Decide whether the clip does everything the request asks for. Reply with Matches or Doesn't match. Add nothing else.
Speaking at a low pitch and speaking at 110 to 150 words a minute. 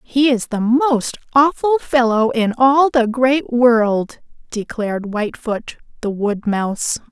Doesn't match